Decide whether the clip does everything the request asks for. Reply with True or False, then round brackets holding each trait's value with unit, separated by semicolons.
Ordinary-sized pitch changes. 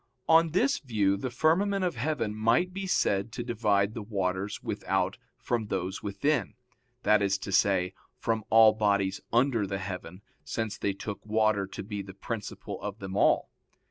True (3.4 semitones)